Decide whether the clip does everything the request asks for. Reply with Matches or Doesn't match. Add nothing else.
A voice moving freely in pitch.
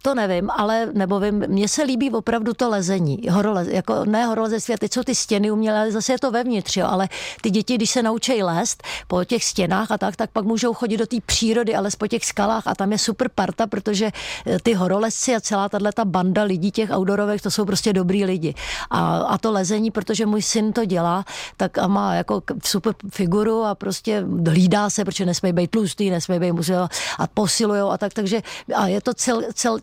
Doesn't match